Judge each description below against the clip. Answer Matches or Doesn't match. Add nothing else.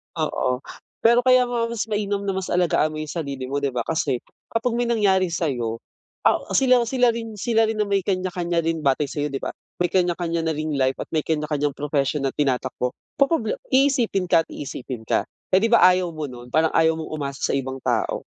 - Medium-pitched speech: Matches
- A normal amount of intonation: Doesn't match